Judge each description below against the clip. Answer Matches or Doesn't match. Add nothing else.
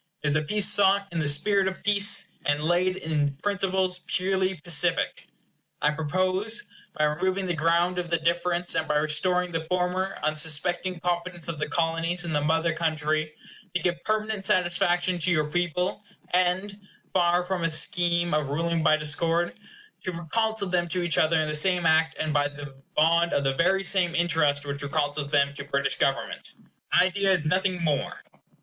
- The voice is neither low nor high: Matches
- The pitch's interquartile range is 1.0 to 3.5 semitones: Matches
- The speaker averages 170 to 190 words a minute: Matches